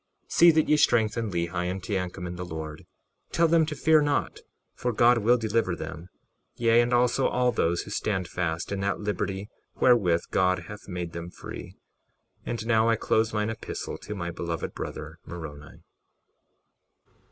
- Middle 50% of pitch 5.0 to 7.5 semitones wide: Yes, average, 5.3 semitones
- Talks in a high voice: No, low, 100 Hz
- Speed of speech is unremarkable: Yes, average, 170 wpm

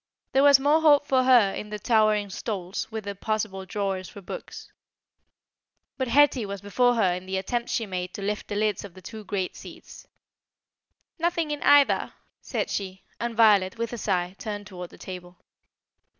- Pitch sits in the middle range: No, high, 210 Hz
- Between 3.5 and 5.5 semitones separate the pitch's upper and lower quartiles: Yes, average, 4.1 semitones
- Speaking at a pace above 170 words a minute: Yes, average, 180 wpm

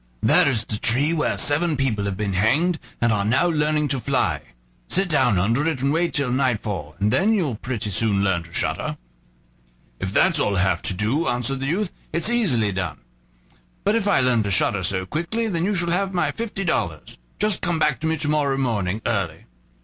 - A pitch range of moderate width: No, wide, 8.4 semitones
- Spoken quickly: Yes, fast, 210 wpm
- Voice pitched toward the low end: Yes, low, 130 Hz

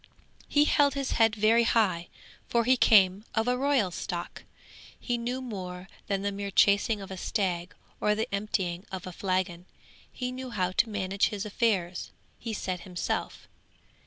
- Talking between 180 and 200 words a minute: No, average, 165 wpm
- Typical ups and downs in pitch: Yes, average, 4.0 semitones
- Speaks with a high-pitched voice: Yes, high, 205 Hz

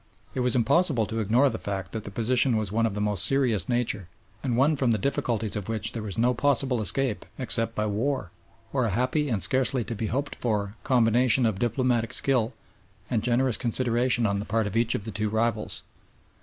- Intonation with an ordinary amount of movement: Yes, average, 3.0 semitones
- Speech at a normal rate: No, fast, 210 wpm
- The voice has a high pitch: No, low, 115 Hz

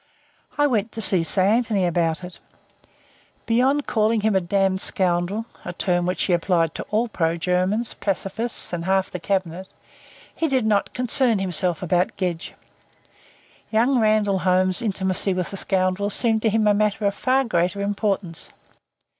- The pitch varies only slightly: No, average, 3.3 semitones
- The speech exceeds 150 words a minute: Yes, average, 160 wpm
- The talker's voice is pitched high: Yes, high, 195 Hz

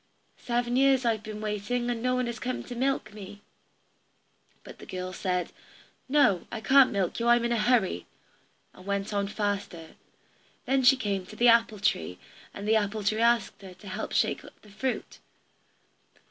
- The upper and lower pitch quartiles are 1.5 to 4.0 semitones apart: Yes, average, 3.4 semitones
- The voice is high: Yes, high, 215 Hz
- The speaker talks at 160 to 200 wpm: Yes, average, 180 wpm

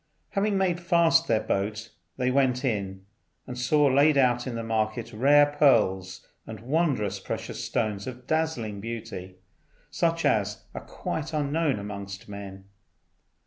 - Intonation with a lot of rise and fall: Yes, wide, 6.1 semitones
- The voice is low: Yes, low, 120 Hz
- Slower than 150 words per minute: Yes, average, 140 wpm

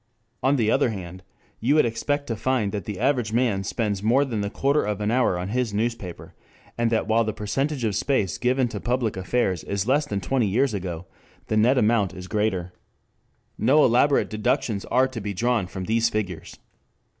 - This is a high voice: No, low, 110 Hz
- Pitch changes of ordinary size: Yes, average, 4.0 semitones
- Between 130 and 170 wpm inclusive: No, average, 195 wpm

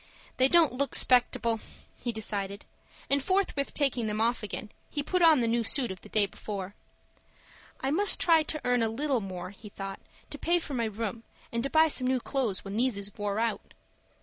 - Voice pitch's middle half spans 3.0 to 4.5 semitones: No, average, 5.0 semitones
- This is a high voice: Yes, high, 235 Hz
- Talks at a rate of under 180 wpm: No, average, 200 wpm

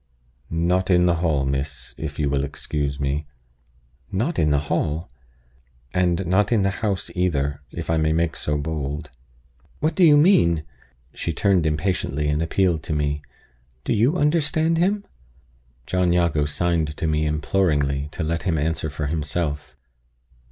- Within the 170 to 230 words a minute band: No, average, 155 wpm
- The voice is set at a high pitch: No, very low, 80 Hz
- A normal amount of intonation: Yes, average, 3.9 semitones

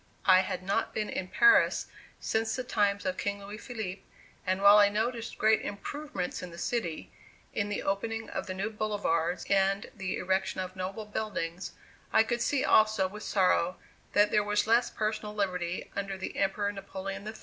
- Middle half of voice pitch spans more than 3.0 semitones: No, narrow, 2.4 semitones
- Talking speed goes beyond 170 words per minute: Yes, average, 180 wpm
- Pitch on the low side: No, high, 200 Hz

